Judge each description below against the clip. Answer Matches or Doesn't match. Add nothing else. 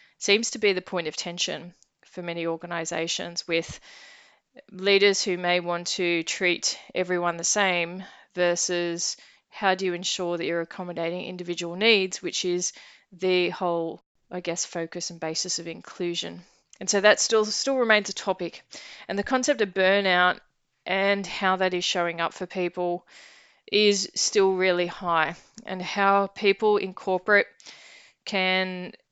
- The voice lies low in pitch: Doesn't match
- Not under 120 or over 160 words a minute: Matches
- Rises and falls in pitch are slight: Matches